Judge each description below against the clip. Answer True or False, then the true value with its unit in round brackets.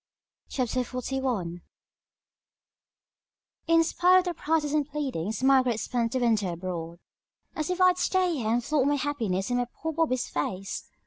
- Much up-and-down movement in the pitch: True (5.9 semitones)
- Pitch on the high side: True (255 Hz)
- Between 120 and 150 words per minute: True (140 wpm)